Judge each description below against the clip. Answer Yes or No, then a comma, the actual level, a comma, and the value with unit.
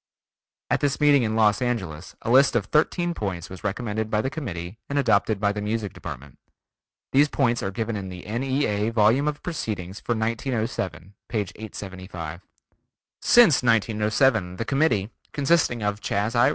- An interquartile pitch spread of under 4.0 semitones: No, average, 4.5 semitones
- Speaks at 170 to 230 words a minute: No, average, 160 wpm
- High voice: No, low, 110 Hz